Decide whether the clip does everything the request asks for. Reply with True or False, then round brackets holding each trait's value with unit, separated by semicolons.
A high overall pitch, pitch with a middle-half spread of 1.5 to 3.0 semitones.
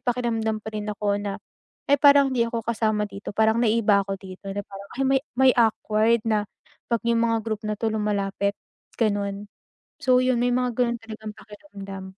True (220 Hz; 2.5 semitones)